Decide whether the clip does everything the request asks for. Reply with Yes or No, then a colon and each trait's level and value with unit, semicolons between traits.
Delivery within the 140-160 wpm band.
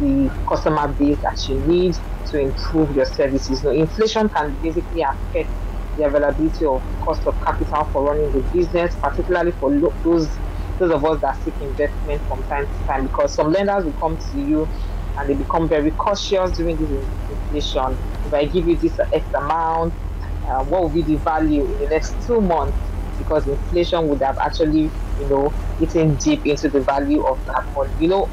No: average, 190 wpm